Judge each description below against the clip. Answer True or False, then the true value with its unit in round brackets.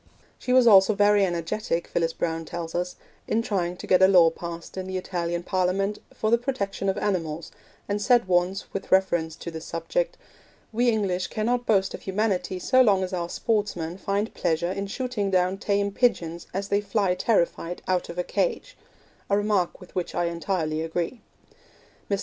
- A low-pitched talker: False (190 Hz)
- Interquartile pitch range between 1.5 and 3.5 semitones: True (3.2 semitones)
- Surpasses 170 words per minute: True (180 wpm)